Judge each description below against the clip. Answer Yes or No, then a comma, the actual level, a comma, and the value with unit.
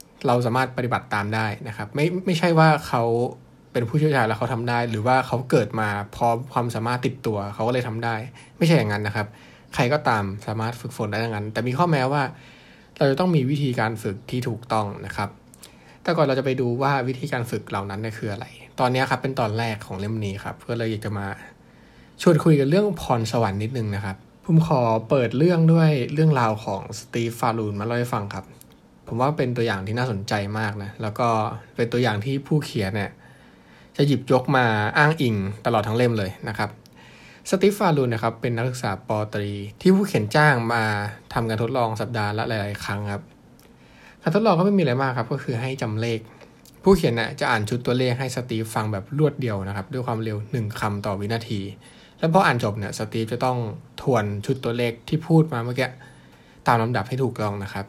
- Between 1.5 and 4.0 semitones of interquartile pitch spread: Yes, average, 3.6 semitones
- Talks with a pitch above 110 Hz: Yes, low, 120 Hz